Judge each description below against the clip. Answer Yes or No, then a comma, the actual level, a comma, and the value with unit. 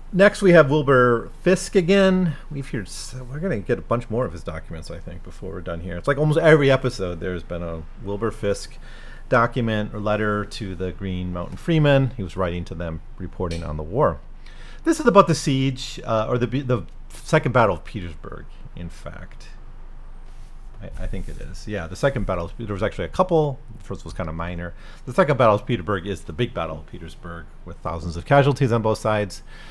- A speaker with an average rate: No, fast, 210 wpm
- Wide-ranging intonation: Yes, wide, 7.4 semitones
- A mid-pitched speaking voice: No, low, 105 Hz